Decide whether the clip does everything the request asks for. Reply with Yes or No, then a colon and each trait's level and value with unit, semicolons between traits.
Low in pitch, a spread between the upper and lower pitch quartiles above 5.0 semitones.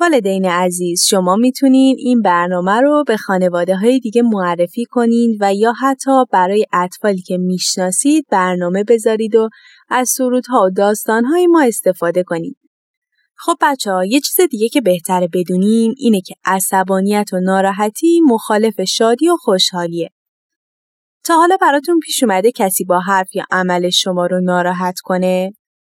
No: high, 210 Hz; wide, 5.4 semitones